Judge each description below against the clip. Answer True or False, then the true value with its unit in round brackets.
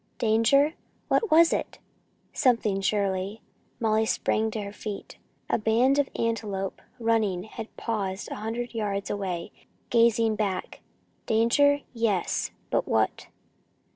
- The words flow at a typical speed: False (120 wpm)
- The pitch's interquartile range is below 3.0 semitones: True (2.5 semitones)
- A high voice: True (220 Hz)